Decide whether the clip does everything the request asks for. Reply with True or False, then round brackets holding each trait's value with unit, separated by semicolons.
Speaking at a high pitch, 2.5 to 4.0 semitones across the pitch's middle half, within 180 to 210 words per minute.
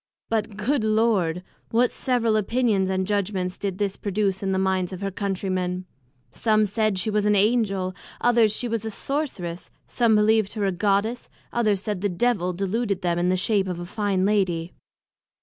True (200 Hz; 2.8 semitones; 185 wpm)